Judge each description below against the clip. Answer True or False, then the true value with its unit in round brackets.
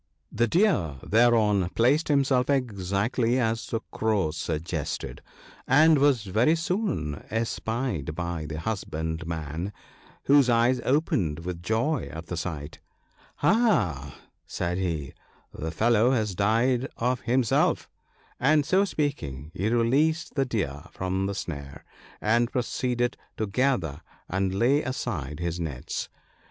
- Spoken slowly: True (130 wpm)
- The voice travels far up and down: True (7.3 semitones)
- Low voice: True (110 Hz)